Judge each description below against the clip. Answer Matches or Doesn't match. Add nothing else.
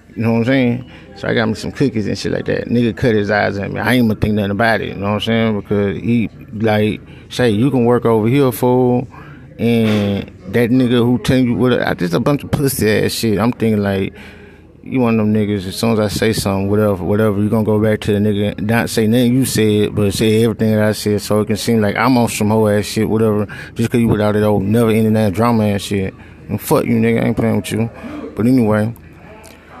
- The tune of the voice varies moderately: Doesn't match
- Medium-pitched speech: Doesn't match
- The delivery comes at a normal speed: Doesn't match